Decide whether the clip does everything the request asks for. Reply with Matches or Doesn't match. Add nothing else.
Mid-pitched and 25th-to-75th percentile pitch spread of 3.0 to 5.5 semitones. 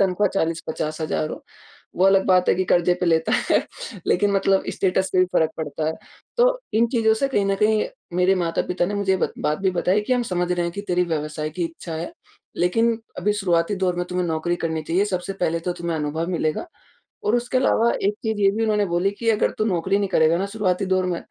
Matches